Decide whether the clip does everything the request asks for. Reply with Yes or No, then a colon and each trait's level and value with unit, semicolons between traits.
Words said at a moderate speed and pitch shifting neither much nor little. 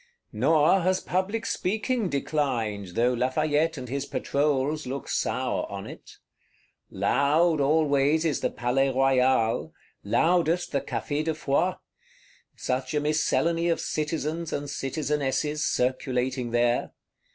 No: slow, 120 wpm; average, 3.5 semitones